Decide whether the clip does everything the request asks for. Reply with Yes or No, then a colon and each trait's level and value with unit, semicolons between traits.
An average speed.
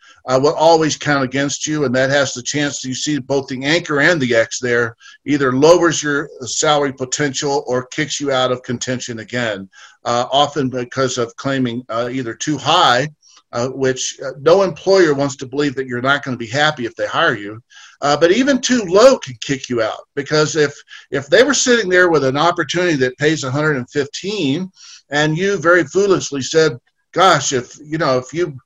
Yes: average, 195 wpm